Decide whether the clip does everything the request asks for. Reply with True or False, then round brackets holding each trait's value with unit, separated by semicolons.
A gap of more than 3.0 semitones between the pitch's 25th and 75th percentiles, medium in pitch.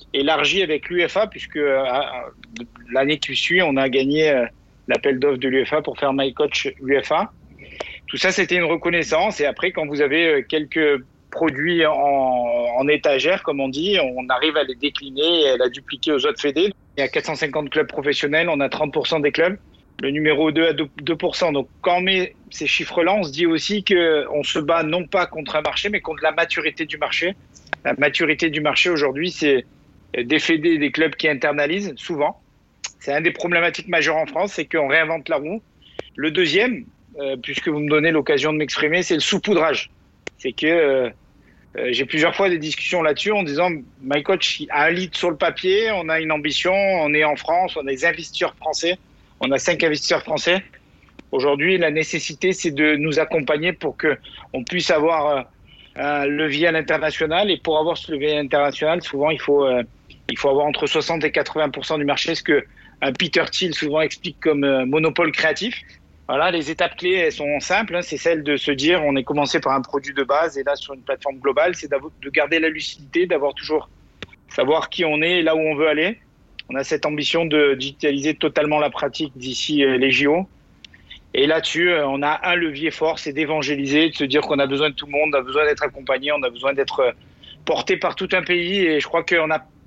False (2.7 semitones; 155 Hz)